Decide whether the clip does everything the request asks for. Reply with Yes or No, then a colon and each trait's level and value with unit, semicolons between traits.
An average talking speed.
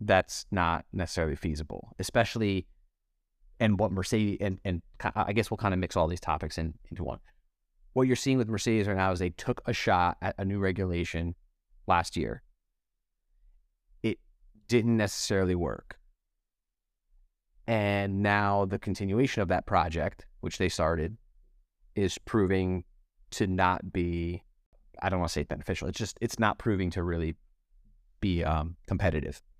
Yes: average, 155 wpm